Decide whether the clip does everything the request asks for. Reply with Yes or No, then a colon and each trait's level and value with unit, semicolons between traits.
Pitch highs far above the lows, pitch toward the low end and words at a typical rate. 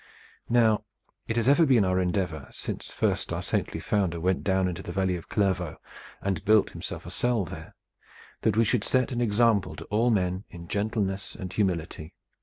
No: average, 3.6 semitones; low, 100 Hz; average, 185 wpm